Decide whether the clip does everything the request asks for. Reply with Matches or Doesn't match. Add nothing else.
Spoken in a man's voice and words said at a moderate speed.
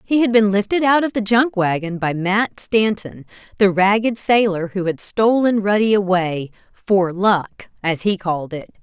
Doesn't match